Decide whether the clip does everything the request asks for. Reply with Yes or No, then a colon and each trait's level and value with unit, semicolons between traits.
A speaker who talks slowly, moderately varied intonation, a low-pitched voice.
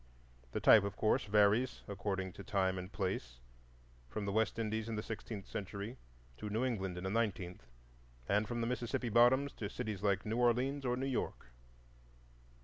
No: average, 175 wpm; average, 3.3 semitones; low, 105 Hz